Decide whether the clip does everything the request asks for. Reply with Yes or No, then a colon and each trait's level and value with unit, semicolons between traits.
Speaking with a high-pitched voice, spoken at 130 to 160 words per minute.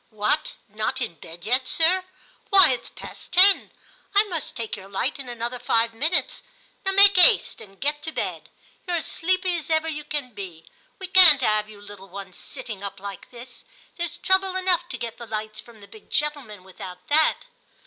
No: very high, 255 Hz; average, 195 wpm